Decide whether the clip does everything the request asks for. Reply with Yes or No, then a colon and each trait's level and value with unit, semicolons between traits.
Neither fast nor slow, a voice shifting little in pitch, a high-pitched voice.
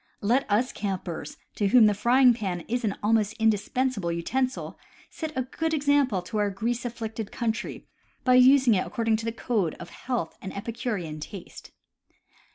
No: average, 165 wpm; average, 4.0 semitones; high, 225 Hz